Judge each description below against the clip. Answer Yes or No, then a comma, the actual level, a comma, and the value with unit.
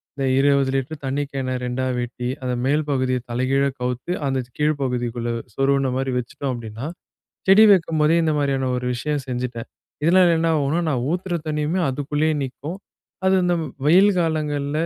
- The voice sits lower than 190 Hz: Yes, medium, 140 Hz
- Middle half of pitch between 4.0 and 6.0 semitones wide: No, average, 3.3 semitones